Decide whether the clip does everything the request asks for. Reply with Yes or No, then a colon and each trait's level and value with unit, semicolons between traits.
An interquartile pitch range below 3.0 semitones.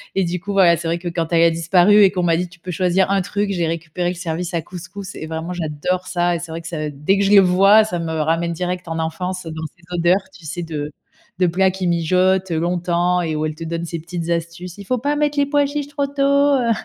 Yes: narrow, 2.4 semitones